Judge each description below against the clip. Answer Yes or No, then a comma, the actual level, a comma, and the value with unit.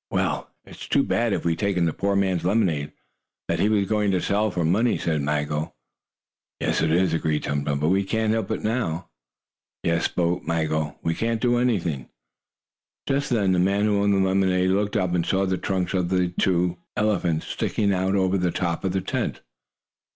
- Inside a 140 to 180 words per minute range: No, average, 195 wpm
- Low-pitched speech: Yes, very low, 95 Hz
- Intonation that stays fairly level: No, average, 3.2 semitones